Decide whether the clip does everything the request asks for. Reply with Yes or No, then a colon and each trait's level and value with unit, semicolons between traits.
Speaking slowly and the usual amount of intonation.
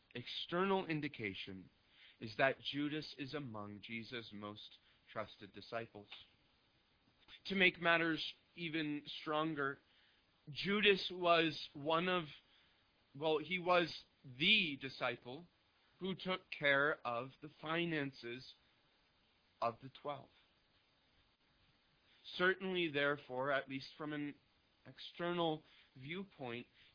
No: slow, 95 wpm; wide, 5.7 semitones